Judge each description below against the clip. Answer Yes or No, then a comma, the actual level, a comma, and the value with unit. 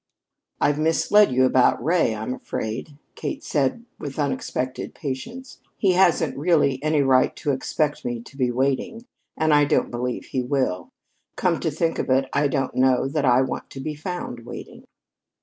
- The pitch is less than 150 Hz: Yes, medium, 140 Hz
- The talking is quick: No, average, 170 wpm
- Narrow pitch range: No, average, 3.4 semitones